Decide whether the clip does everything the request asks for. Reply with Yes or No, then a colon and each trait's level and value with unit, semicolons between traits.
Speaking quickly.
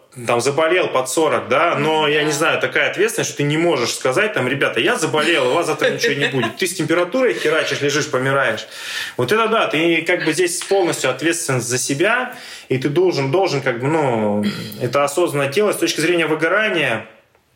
Yes: fast, 195 wpm